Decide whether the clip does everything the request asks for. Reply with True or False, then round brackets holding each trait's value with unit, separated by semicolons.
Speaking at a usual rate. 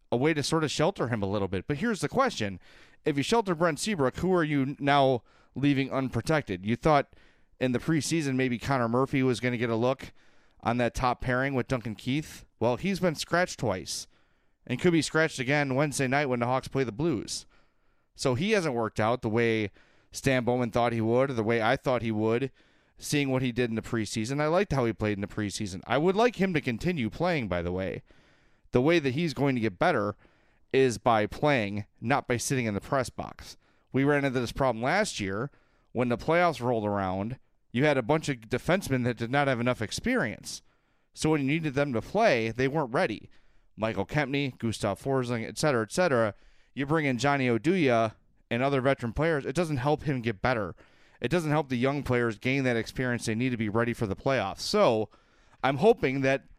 False (215 wpm)